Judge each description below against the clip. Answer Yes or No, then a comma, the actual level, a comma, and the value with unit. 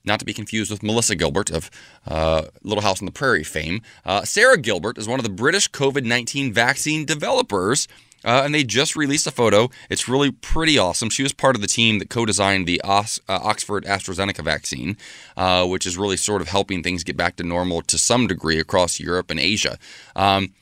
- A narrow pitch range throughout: No, average, 4.7 semitones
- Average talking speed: No, fast, 210 wpm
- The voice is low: Yes, low, 100 Hz